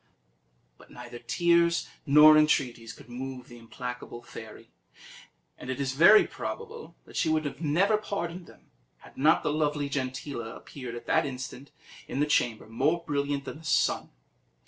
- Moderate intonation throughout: Yes, average, 4.1 semitones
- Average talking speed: Yes, average, 160 wpm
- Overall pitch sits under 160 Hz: Yes, medium, 140 Hz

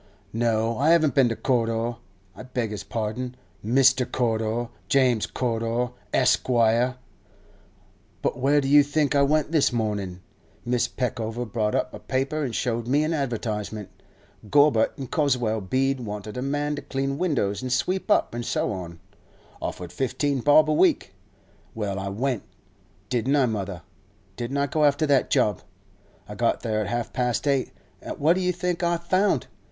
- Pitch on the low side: Yes, low, 125 Hz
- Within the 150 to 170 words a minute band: Yes, average, 160 wpm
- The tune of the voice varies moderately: Yes, average, 4.2 semitones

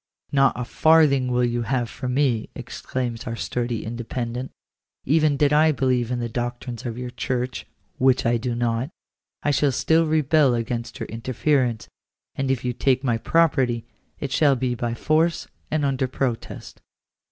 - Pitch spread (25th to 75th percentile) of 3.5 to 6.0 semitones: No, average, 2.8 semitones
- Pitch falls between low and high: No, low, 125 Hz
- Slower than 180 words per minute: Yes, average, 170 wpm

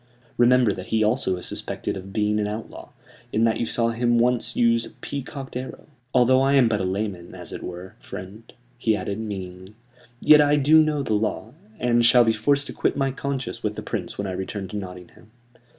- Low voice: Yes, low, 115 Hz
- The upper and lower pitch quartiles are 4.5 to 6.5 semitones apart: No, average, 4.0 semitones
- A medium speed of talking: No, fast, 210 wpm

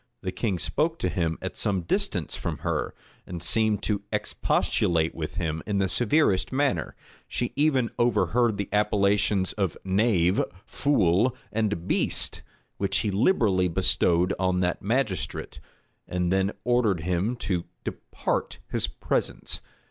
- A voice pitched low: Yes, low, 100 Hz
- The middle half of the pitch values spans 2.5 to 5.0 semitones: Yes, average, 3.9 semitones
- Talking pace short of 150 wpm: Yes, slow, 135 wpm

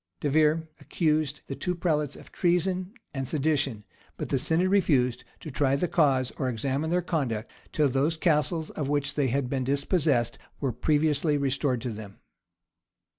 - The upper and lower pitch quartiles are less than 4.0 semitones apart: Yes, average, 3.2 semitones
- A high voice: No, medium, 145 Hz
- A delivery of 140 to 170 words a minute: Yes, average, 165 wpm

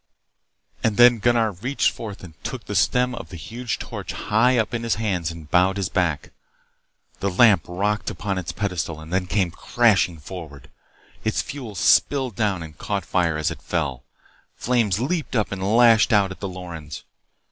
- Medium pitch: No, low, 100 Hz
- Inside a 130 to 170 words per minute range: No, average, 180 wpm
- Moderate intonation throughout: Yes, average, 4.8 semitones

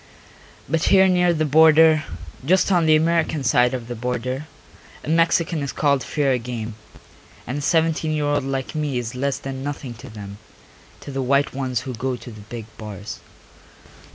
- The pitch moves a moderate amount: Yes, average, 4.1 semitones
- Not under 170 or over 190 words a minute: Yes, average, 180 wpm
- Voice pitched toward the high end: No, low, 135 Hz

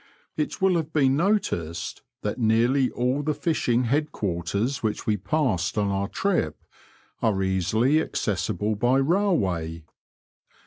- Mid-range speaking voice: No, low, 120 Hz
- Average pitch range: No, wide, 7.3 semitones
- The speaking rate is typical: No, slow, 130 wpm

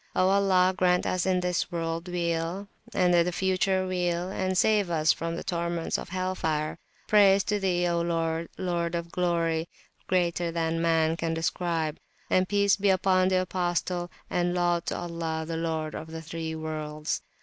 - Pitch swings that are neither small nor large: No, narrow, 1.9 semitones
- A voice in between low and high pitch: Yes, medium, 175 Hz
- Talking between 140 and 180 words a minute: Yes, average, 175 wpm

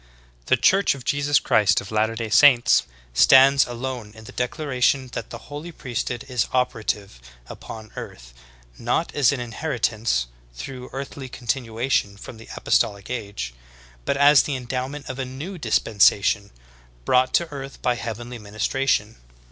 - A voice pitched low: Yes, low, 125 Hz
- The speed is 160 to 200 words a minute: No, average, 150 wpm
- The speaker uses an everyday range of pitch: Yes, average, 3.7 semitones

